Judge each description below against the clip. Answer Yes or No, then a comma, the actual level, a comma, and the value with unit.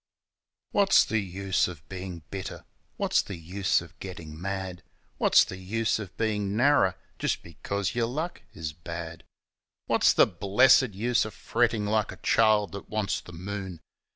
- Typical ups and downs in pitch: Yes, average, 3.5 semitones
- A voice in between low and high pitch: No, low, 100 Hz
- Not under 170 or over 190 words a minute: No, average, 155 wpm